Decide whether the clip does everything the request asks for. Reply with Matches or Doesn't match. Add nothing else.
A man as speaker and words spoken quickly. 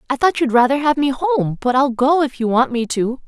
Doesn't match